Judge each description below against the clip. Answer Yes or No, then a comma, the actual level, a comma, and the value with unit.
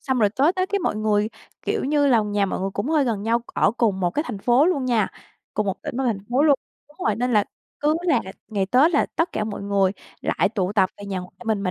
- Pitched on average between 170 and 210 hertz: No, high, 220 Hz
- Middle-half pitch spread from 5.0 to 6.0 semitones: Yes, wide, 5.6 semitones